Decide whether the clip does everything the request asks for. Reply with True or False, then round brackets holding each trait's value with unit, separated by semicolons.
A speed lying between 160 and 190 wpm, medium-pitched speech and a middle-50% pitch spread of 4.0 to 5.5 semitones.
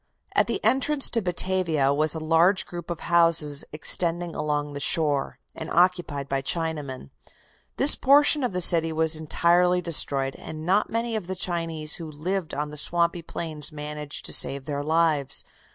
False (170 wpm; 165 Hz; 3.1 semitones)